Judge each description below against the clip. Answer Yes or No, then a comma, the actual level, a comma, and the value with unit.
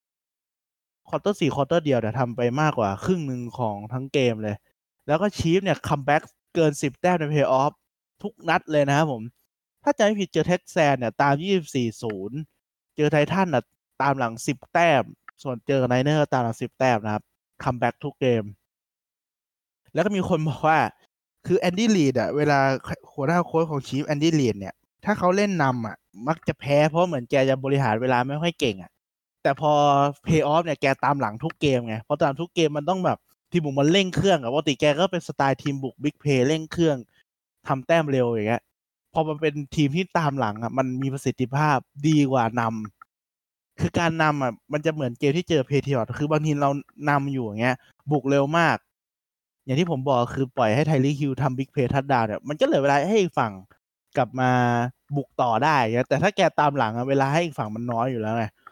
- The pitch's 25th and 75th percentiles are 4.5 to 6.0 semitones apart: No, average, 4.0 semitones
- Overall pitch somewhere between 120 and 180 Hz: Yes, medium, 140 Hz